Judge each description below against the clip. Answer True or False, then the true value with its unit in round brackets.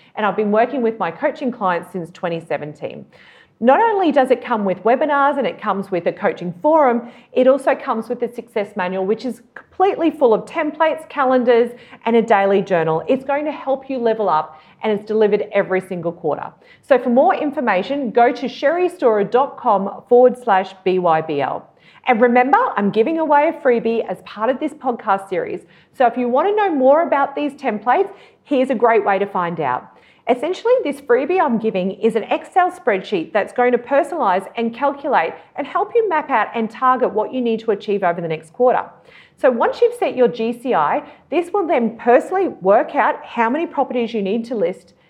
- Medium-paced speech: True (195 wpm)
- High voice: True (245 Hz)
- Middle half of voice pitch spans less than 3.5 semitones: False (5.4 semitones)